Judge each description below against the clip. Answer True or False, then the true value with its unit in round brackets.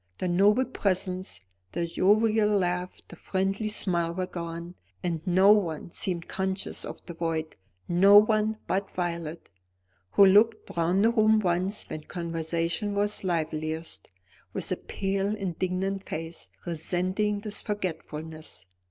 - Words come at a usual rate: False (130 wpm)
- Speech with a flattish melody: False (3.3 semitones)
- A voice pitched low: False (185 Hz)